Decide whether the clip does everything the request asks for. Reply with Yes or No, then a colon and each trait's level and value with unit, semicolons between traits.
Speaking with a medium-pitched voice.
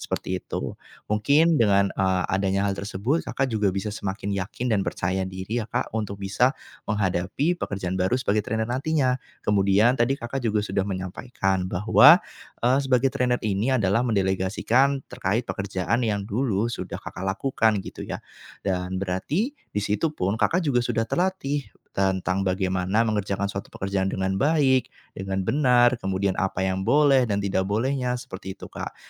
No: low, 105 Hz